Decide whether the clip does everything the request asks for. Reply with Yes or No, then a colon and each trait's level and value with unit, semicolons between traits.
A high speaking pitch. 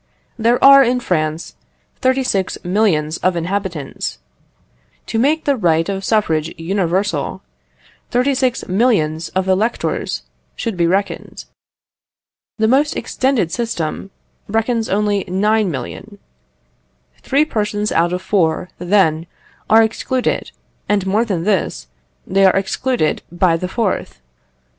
Yes: high, 200 Hz